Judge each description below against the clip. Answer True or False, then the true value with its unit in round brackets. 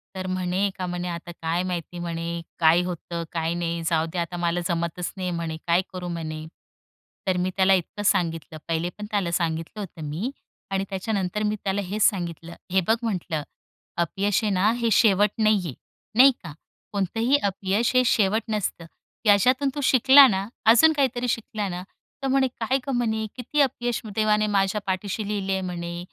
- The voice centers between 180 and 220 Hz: True (190 Hz)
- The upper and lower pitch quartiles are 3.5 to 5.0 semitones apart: True (4.0 semitones)